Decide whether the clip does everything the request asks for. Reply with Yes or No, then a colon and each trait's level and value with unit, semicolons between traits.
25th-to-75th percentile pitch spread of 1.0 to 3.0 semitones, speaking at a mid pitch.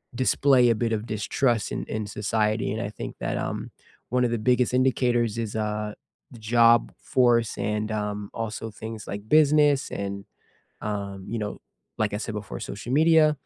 No: narrow, 2.6 semitones; low, 110 Hz